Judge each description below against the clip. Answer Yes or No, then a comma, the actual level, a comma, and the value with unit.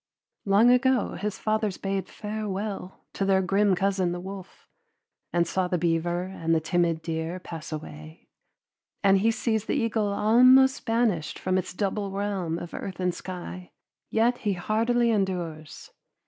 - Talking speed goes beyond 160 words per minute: No, average, 150 wpm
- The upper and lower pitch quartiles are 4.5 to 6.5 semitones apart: No, average, 3.6 semitones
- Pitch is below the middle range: No, high, 190 Hz